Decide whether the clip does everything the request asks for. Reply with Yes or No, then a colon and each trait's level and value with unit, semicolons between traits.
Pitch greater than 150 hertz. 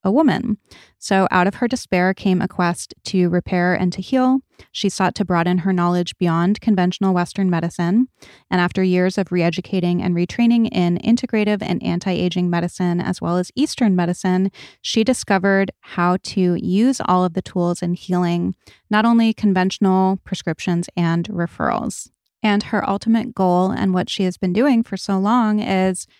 Yes: medium, 185 Hz